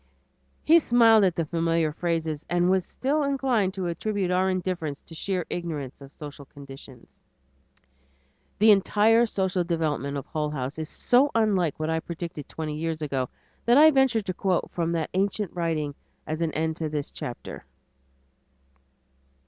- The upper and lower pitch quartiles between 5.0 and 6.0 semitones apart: No, average, 4.5 semitones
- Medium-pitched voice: Yes, medium, 170 Hz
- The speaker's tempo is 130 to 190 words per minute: Yes, average, 155 wpm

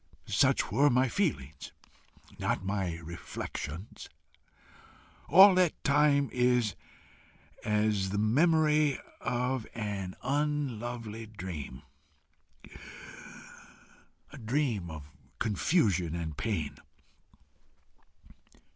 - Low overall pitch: Yes, low, 110 Hz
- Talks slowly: Yes, slow, 75 wpm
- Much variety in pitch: Yes, wide, 7.2 semitones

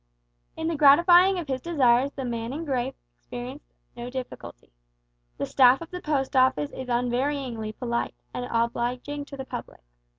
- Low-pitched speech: No, very high, 260 Hz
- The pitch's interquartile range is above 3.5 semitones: No, average, 3.1 semitones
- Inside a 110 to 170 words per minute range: Yes, average, 160 wpm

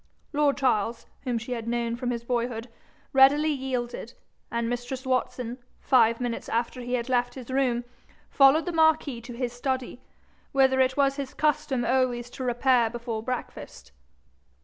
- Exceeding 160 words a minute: No, average, 155 wpm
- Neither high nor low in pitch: No, very high, 250 Hz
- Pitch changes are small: Yes, narrow, 2.0 semitones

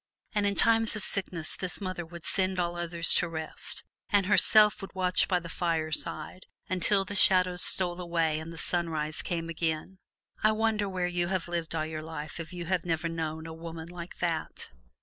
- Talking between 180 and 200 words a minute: Yes, average, 190 wpm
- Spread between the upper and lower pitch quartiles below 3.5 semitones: Yes, narrow, 2.4 semitones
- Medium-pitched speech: Yes, medium, 175 Hz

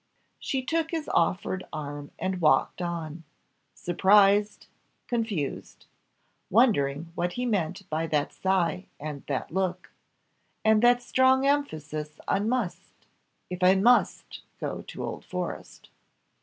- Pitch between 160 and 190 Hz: Yes, medium, 185 Hz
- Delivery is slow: Yes, slow, 120 wpm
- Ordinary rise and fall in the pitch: No, wide, 6.6 semitones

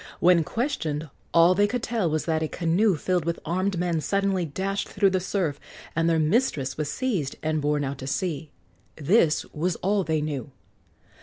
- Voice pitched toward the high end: No, medium, 170 Hz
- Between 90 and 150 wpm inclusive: No, average, 180 wpm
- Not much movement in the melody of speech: No, average, 4.2 semitones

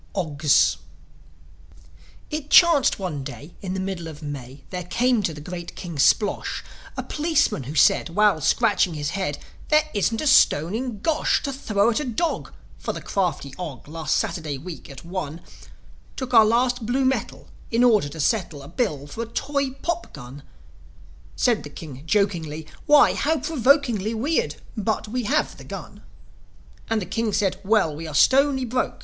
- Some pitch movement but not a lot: No, wide, 8.0 semitones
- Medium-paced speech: Yes, average, 170 wpm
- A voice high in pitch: Yes, high, 200 Hz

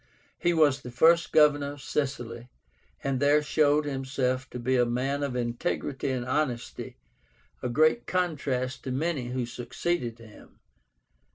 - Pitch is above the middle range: No, low, 135 Hz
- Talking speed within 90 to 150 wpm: Yes, average, 145 wpm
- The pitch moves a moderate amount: Yes, average, 3.2 semitones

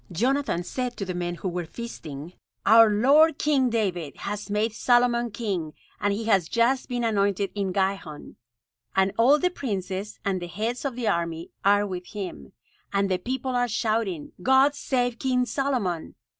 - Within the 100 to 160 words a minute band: No, average, 170 wpm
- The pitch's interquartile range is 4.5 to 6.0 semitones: Yes, average, 4.9 semitones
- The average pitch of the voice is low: No, high, 210 Hz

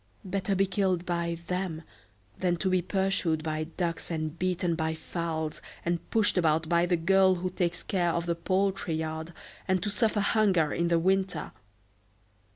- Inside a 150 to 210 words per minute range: Yes, average, 160 wpm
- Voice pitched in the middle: Yes, medium, 175 Hz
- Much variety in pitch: No, narrow, 2.5 semitones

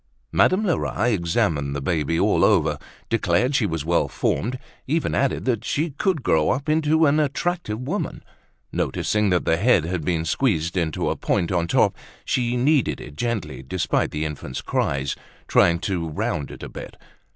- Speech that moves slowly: No, average, 170 wpm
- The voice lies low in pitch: Yes, low, 100 Hz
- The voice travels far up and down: Yes, wide, 8.8 semitones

